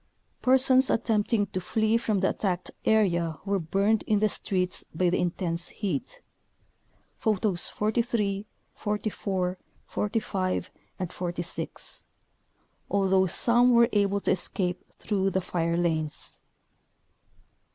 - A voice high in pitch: Yes, high, 195 Hz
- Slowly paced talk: Yes, slow, 110 wpm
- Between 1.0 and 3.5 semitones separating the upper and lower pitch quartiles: Yes, average, 3.2 semitones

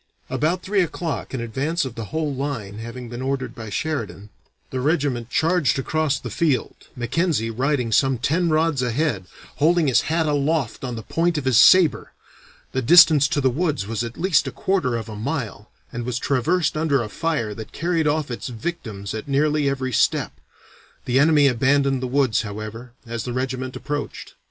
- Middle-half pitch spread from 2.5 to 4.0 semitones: No, average, 4.8 semitones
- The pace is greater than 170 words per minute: Yes, average, 180 wpm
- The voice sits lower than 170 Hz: Yes, low, 135 Hz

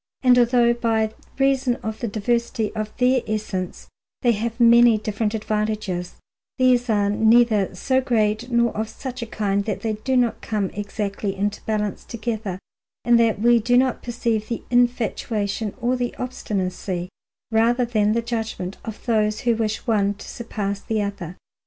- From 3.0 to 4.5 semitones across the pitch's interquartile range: No, narrow, 2.4 semitones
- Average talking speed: Yes, average, 160 wpm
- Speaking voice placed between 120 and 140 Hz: No, high, 220 Hz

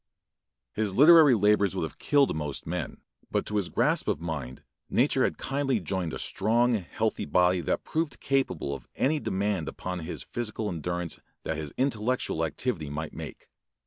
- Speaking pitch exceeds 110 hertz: No, low, 100 Hz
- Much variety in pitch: Yes, wide, 7.0 semitones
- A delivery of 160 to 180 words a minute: Yes, average, 165 wpm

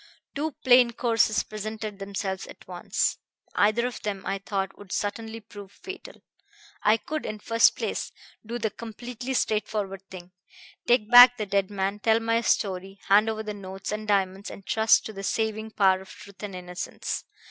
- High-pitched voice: Yes, high, 210 Hz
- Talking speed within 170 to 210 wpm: Yes, average, 175 wpm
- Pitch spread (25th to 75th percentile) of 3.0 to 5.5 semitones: No, narrow, 2.5 semitones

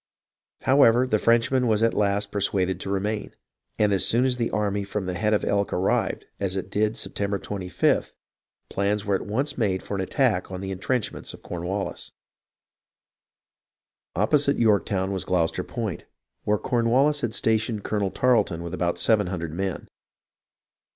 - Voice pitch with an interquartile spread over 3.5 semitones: No, average, 3.2 semitones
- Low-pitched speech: Yes, low, 105 Hz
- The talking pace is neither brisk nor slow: Yes, average, 165 wpm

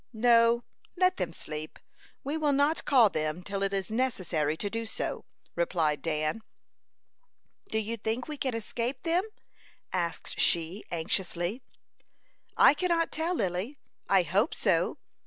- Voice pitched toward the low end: No, high, 215 Hz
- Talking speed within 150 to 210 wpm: No, average, 140 wpm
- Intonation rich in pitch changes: Yes, wide, 7.5 semitones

